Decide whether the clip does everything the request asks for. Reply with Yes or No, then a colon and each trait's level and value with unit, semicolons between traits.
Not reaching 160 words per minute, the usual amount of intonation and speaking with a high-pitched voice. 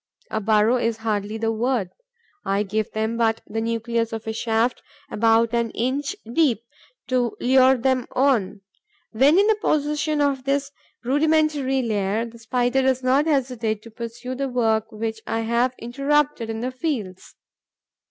Yes: average, 150 wpm; average, 3.1 semitones; high, 235 Hz